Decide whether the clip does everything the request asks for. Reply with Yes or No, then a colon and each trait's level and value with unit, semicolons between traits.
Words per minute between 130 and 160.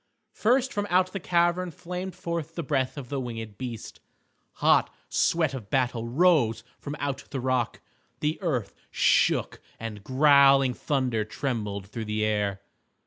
Yes: average, 145 wpm